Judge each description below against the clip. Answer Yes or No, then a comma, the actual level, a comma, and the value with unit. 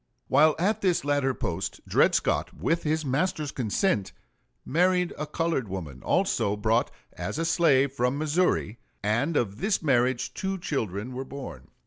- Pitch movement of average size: No, wide, 6.2 semitones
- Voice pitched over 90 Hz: Yes, medium, 140 Hz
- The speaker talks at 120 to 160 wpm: Yes, average, 150 wpm